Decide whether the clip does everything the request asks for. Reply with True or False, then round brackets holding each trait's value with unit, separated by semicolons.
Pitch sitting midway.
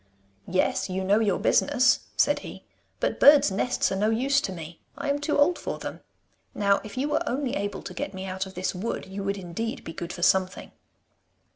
False (200 Hz)